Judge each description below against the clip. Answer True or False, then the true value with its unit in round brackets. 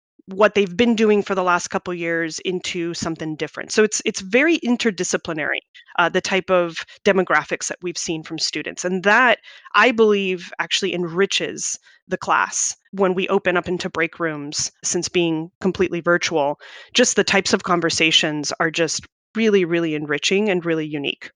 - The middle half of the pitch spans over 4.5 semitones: False (3.2 semitones)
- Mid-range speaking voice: True (180 Hz)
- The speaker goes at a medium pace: True (170 wpm)